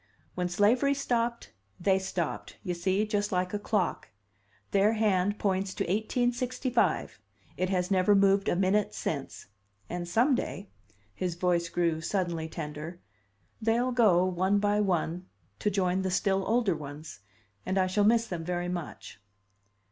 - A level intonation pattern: No, average, 3.0 semitones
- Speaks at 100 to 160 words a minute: Yes, average, 150 wpm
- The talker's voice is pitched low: No, high, 190 Hz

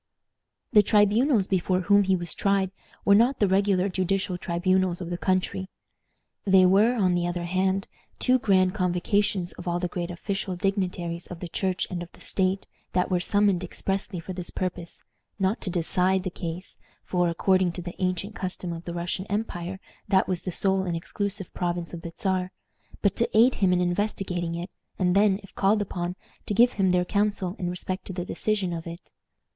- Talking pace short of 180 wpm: No, average, 190 wpm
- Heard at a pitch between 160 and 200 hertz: Yes, medium, 185 Hz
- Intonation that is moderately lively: No, narrow, 1.9 semitones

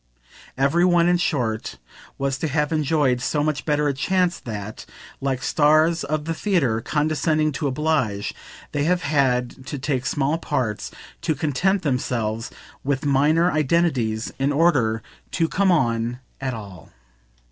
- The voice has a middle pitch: Yes, medium, 145 Hz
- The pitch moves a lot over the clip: No, average, 4.0 semitones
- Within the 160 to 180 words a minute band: No, average, 145 wpm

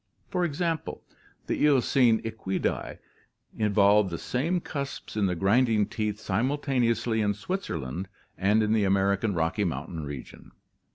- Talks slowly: Yes, slow, 130 wpm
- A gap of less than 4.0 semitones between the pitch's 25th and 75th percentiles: No, average, 4.8 semitones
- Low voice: Yes, low, 105 Hz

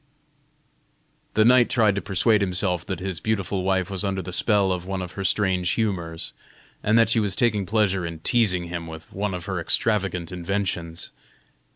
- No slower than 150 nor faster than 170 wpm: No, average, 180 wpm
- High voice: No, very low, 95 Hz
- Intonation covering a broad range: No, average, 2.7 semitones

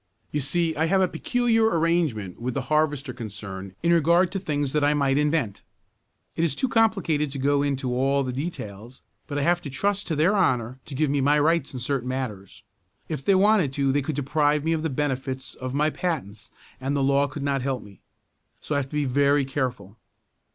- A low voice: No, medium, 145 Hz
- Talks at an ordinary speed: No, fast, 215 wpm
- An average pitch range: Yes, average, 3.6 semitones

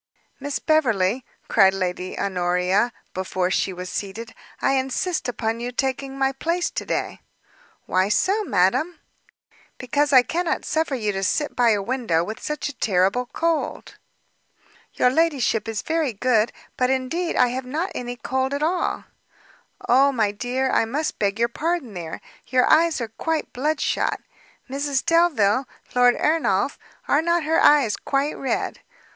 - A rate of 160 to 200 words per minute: No, average, 150 wpm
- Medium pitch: No, very high, 255 Hz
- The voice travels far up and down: Yes, wide, 5.9 semitones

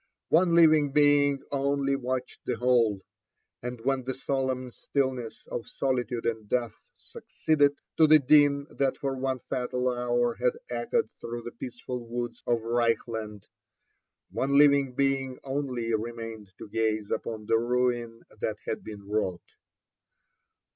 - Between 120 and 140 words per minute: Yes, slow, 135 wpm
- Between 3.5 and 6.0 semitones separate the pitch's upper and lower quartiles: No, average, 3.0 semitones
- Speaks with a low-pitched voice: Yes, low, 125 Hz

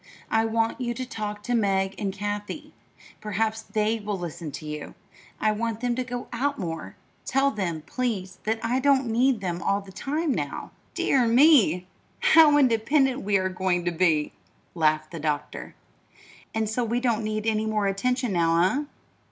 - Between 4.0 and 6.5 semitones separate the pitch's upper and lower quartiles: Yes, average, 4.7 semitones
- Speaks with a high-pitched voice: Yes, high, 215 Hz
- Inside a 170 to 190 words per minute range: Yes, average, 175 wpm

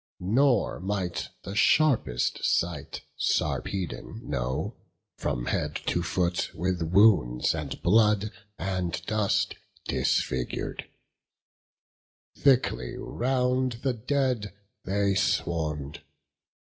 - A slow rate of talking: Yes, slow, 85 wpm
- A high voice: No, very low, 95 Hz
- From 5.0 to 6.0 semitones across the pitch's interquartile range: Yes, wide, 5.4 semitones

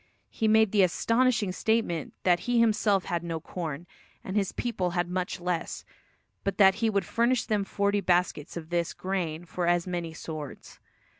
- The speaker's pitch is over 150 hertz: Yes, medium, 185 Hz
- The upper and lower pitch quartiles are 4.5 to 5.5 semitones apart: No, average, 3.4 semitones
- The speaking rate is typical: Yes, average, 170 wpm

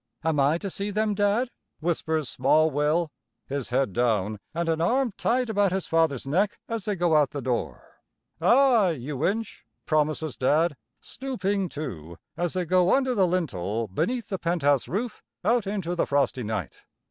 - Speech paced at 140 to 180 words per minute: Yes, average, 170 wpm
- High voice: No, medium, 165 Hz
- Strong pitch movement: Yes, wide, 6.3 semitones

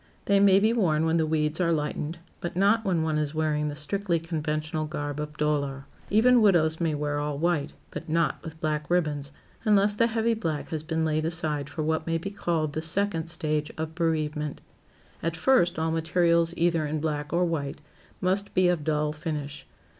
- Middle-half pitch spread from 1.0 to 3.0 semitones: Yes, narrow, 2.5 semitones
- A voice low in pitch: No, medium, 160 Hz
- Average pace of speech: Yes, average, 190 wpm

